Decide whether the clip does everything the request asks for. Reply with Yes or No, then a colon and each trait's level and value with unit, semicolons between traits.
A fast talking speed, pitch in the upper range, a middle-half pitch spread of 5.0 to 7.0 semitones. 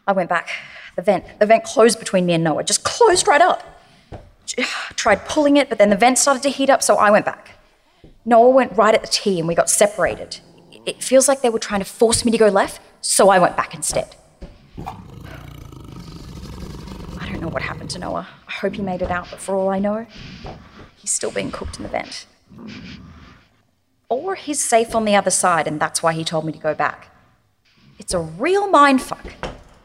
Yes: fast, 210 wpm; high, 215 Hz; wide, 5.6 semitones